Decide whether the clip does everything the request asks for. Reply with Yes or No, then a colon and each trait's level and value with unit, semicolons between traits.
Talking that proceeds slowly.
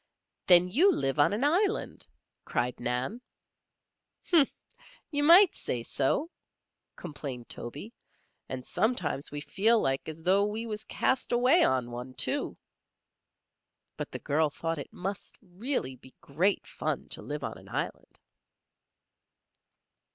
Yes: slow, 130 wpm